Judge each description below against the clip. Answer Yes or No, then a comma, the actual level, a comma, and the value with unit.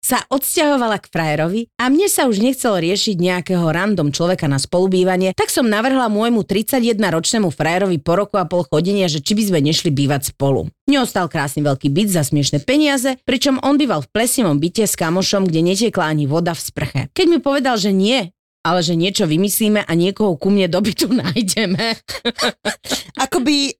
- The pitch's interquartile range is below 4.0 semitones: No, wide, 6.3 semitones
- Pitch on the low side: No, high, 195 Hz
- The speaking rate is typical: No, fast, 180 wpm